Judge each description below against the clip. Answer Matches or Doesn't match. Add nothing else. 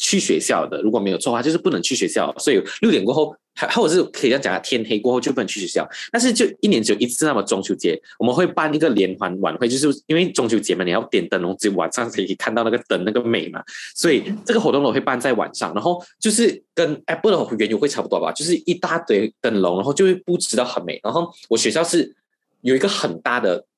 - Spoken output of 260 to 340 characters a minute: Doesn't match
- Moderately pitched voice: Matches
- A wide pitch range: Matches